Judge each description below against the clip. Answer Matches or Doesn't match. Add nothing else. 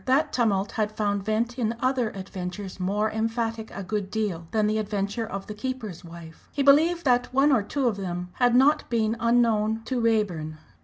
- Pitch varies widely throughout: Doesn't match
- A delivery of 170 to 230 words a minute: Matches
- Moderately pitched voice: Doesn't match